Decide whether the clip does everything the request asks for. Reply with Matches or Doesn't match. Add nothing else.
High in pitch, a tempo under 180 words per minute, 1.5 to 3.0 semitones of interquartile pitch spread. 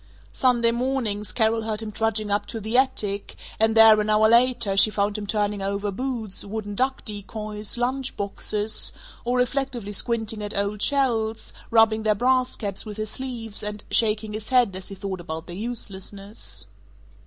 Matches